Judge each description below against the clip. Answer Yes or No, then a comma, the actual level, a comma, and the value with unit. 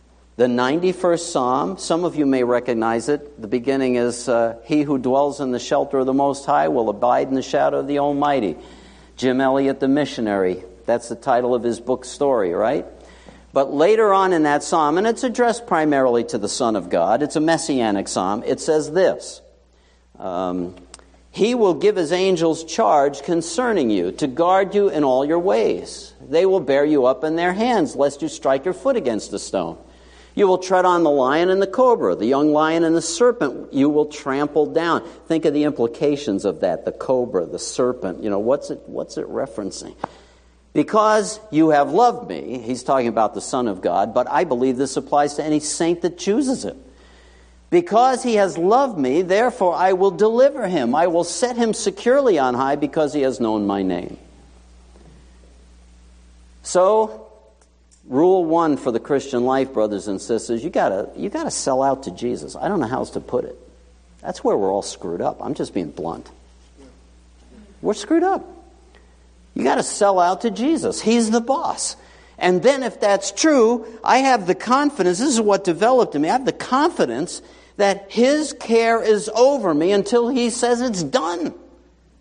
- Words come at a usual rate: Yes, average, 190 wpm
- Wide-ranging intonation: Yes, wide, 8.7 semitones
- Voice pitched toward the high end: No, medium, 145 Hz